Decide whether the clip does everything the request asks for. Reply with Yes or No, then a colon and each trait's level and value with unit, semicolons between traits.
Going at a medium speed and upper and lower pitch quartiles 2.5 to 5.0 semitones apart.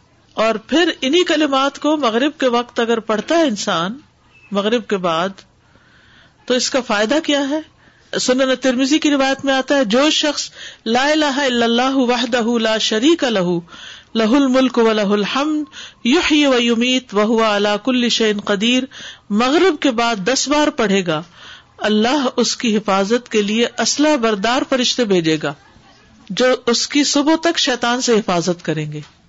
Yes: average, 160 wpm; average, 4.5 semitones